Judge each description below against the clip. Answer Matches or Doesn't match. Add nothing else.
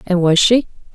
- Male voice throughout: Doesn't match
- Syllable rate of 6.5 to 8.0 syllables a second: Doesn't match